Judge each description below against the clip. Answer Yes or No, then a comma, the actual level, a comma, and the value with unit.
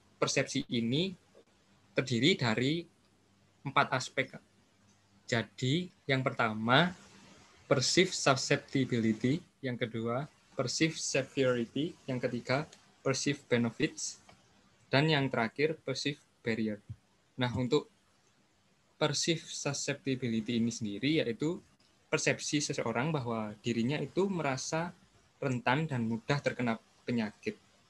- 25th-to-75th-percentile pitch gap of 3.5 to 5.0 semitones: Yes, average, 4.4 semitones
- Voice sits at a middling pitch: No, low, 130 Hz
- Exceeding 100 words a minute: No, average, 90 wpm